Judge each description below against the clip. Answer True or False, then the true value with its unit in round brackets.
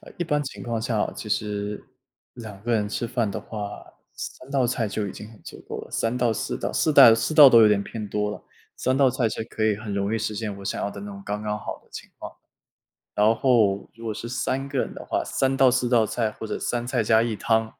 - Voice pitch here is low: True (115 Hz)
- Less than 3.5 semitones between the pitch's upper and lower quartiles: True (2.8 semitones)